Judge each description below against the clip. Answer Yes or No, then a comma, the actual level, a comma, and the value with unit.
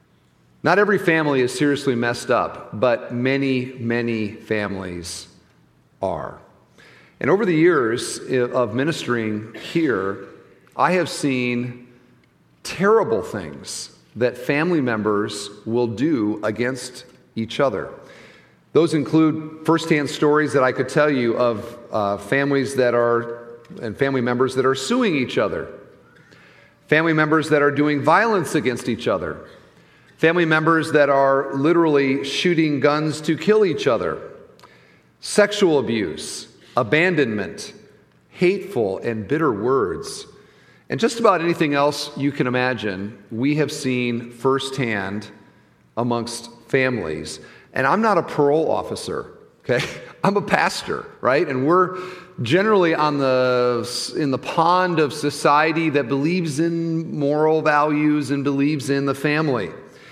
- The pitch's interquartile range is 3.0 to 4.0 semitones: No, average, 4.8 semitones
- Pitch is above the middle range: No, medium, 140 Hz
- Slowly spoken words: Yes, slow, 125 wpm